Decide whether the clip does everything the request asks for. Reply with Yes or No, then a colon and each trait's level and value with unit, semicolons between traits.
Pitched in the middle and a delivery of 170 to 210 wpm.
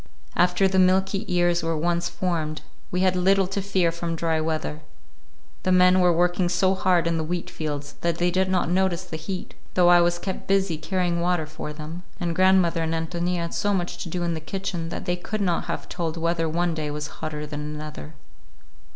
Yes: medium, 175 Hz; average, 200 wpm